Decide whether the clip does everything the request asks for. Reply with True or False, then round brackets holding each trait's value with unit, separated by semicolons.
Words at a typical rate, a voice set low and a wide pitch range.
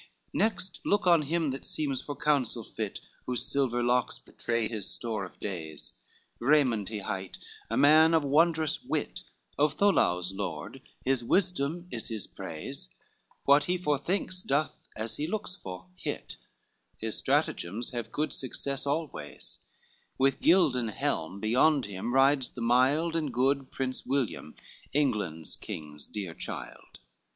True (145 wpm; 130 Hz; 5.8 semitones)